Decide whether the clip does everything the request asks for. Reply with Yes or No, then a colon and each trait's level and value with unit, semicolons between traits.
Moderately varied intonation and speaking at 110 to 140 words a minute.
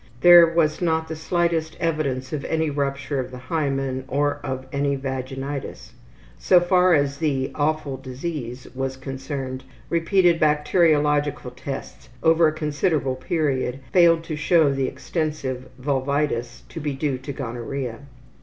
Yes: average, 3.3 semitones; slow, 135 wpm